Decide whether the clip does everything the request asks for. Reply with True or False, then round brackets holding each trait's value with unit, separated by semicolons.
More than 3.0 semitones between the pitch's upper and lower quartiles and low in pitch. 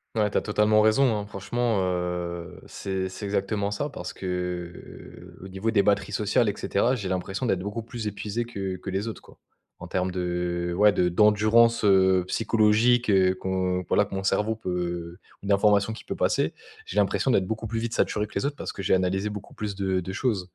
False (2.7 semitones; 100 Hz)